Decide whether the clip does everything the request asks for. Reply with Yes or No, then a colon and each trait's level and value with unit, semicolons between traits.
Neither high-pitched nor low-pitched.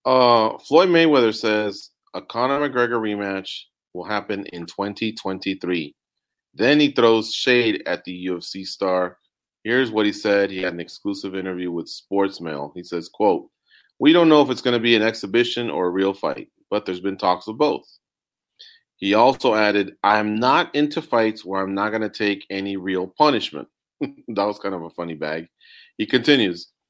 No: low, 105 Hz